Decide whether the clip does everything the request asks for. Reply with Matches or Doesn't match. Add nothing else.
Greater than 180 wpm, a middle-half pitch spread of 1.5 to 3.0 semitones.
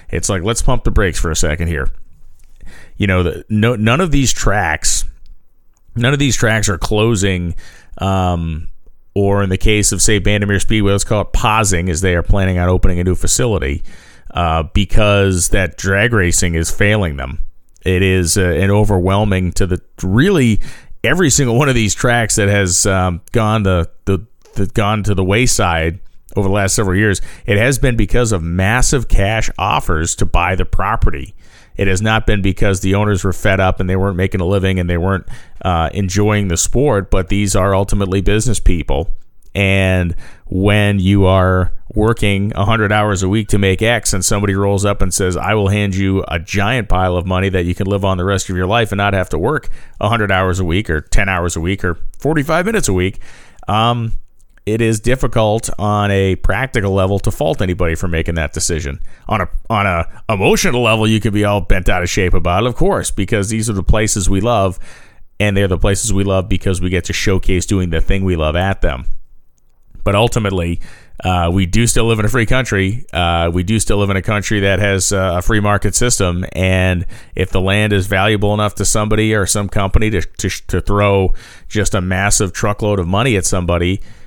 Matches